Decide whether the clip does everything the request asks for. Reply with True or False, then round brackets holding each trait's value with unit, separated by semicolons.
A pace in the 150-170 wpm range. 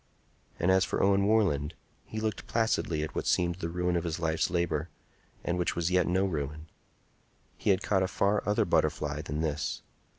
False (190 wpm)